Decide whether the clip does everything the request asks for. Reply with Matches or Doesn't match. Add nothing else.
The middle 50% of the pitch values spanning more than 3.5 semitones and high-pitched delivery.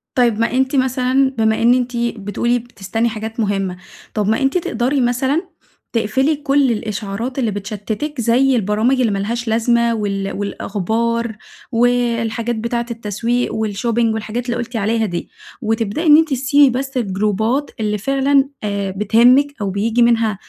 Doesn't match